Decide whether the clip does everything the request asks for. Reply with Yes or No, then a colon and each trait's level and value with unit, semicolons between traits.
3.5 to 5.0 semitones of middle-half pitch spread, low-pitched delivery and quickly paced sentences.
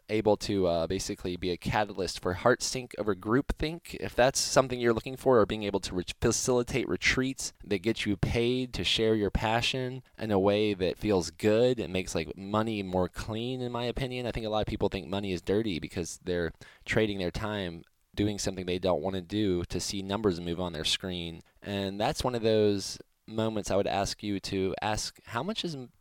Yes: average, 3.8 semitones; low, 105 Hz; fast, 215 wpm